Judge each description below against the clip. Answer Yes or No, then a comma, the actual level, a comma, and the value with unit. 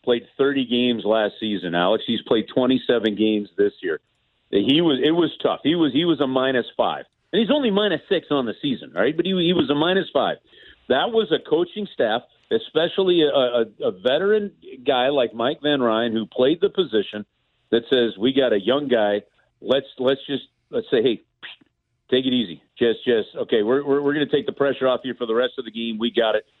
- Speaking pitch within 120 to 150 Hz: Yes, low, 135 Hz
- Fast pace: Yes, fast, 220 wpm